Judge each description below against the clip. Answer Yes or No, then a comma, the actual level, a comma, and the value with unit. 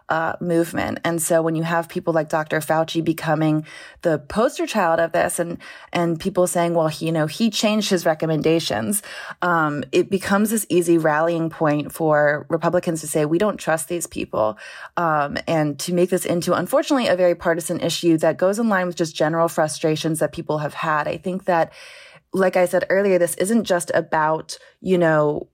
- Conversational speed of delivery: Yes, average, 190 wpm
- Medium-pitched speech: Yes, medium, 170 Hz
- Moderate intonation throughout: No, narrow, 2.3 semitones